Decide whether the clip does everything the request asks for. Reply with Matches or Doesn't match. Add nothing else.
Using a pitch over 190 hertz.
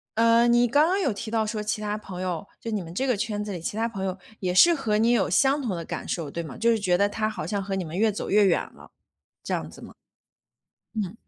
Matches